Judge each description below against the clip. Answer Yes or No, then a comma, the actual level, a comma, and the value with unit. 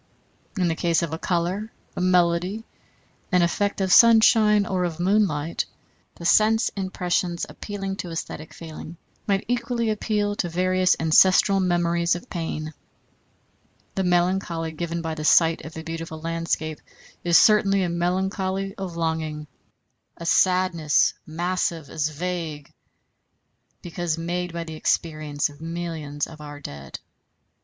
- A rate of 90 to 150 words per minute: Yes, slow, 135 wpm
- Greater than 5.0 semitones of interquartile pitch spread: No, average, 2.8 semitones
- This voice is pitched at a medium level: Yes, medium, 175 Hz